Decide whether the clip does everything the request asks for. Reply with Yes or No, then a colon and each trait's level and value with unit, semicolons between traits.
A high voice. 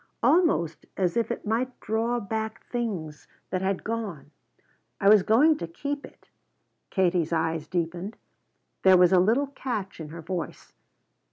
Yes: high, 195 Hz